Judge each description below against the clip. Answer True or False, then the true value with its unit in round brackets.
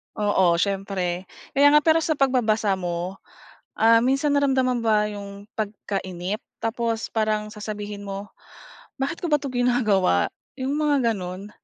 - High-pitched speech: True (215 Hz)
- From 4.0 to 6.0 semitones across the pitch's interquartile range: True (4.5 semitones)